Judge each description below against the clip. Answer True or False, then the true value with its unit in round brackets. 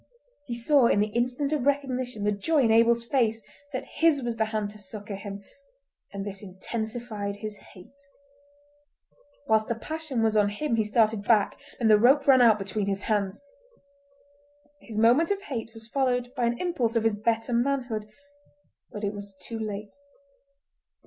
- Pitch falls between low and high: False (225 Hz)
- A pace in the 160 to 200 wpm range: True (170 wpm)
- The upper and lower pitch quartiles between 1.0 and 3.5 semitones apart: True (3.1 semitones)